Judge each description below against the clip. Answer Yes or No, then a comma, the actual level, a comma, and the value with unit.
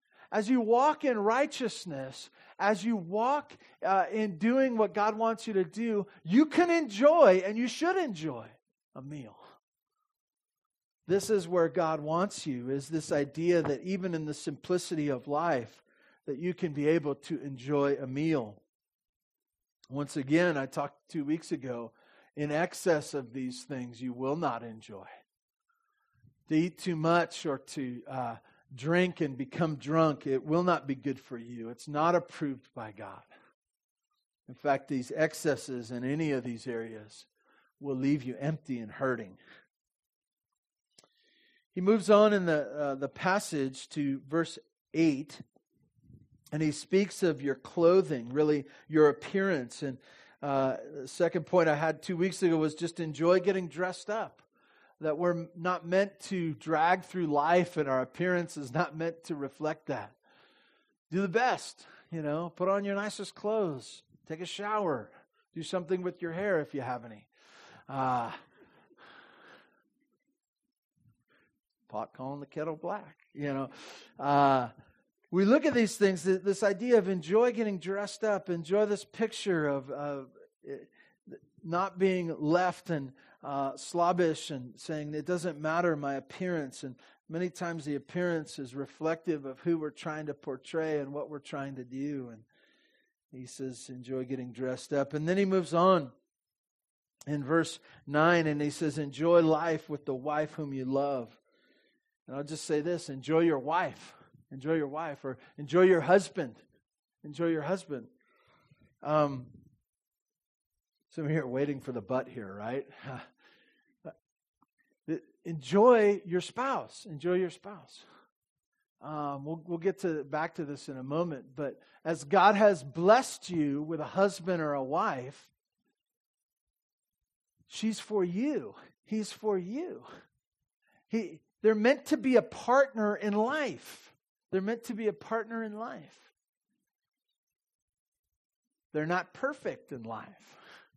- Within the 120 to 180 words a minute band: Yes, average, 150 wpm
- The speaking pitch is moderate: Yes, medium, 165 Hz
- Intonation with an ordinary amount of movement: No, wide, 5.7 semitones